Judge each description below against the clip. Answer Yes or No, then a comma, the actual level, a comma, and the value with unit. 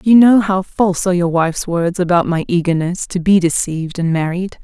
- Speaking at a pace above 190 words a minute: Yes, fast, 205 wpm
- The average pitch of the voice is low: No, medium, 180 Hz